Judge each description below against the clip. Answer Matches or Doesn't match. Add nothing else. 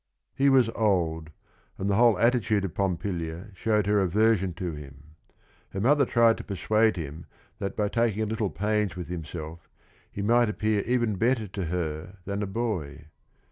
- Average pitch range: Matches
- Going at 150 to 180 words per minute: Matches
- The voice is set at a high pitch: Doesn't match